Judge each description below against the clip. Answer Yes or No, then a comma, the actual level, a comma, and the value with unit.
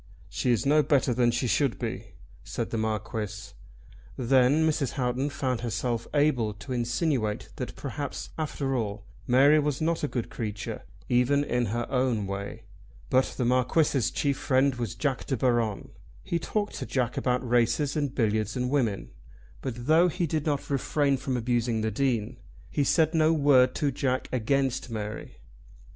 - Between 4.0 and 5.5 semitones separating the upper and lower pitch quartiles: No, average, 3.5 semitones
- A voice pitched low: Yes, low, 125 Hz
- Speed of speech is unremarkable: Yes, average, 165 wpm